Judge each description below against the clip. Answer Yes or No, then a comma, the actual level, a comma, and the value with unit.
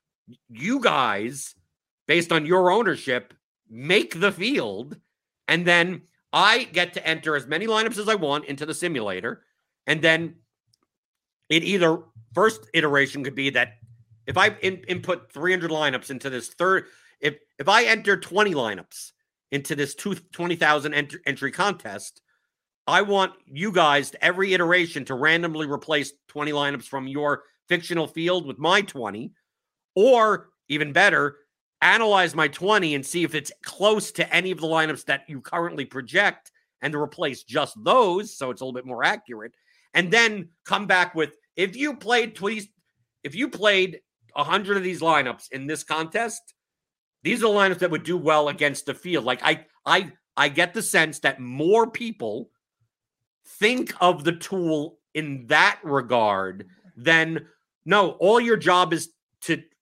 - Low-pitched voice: No, medium, 165 Hz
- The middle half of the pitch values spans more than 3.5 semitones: Yes, average, 4.8 semitones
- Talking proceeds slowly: No, average, 160 wpm